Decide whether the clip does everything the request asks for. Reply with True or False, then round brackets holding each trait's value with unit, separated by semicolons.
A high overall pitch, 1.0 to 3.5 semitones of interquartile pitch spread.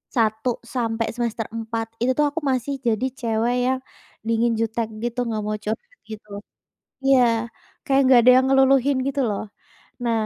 True (235 Hz; 2.7 semitones)